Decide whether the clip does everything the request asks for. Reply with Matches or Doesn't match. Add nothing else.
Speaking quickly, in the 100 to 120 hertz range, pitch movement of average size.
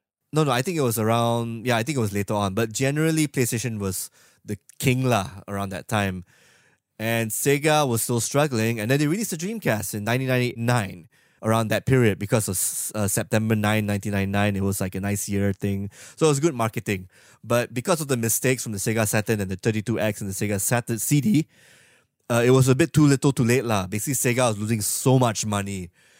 Matches